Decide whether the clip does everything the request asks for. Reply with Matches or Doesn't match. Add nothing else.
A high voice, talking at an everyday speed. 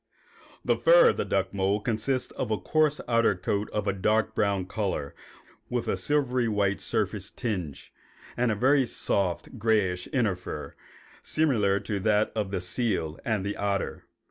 Doesn't match